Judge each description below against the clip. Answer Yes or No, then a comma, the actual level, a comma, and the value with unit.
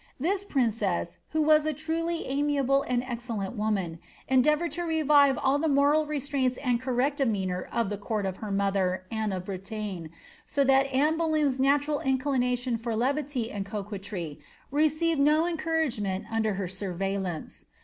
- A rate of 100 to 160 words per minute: Yes, average, 155 wpm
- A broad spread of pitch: Yes, wide, 6.4 semitones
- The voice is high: Yes, very high, 255 Hz